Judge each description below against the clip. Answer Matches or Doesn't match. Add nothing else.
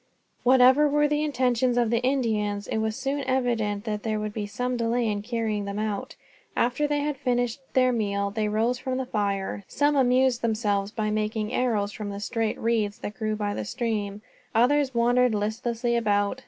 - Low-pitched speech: Doesn't match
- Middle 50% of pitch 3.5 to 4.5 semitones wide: Doesn't match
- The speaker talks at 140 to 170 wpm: Doesn't match